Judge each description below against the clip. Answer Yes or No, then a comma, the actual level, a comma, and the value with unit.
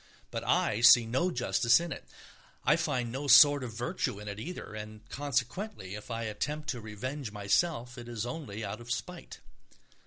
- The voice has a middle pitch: No, low, 120 Hz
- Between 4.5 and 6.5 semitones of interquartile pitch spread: Yes, average, 4.8 semitones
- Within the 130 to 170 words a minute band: No, average, 180 wpm